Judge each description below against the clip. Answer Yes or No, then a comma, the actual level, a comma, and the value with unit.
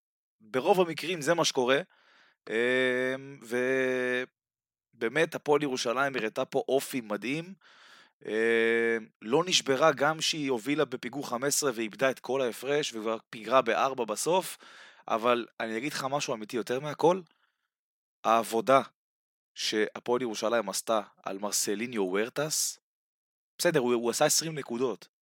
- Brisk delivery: No, average, 115 wpm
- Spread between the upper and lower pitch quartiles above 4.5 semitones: No, average, 3.9 semitones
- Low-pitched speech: Yes, low, 130 Hz